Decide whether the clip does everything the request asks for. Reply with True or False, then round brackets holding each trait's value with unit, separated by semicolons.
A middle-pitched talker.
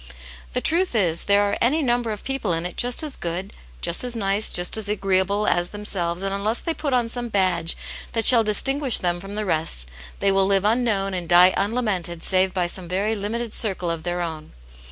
False (200 Hz)